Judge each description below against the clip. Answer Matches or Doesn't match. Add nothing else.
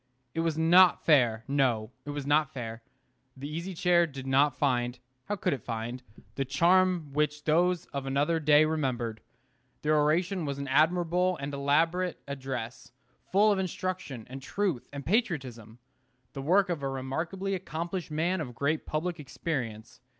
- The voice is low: Doesn't match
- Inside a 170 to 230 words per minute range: Doesn't match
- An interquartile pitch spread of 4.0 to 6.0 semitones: Matches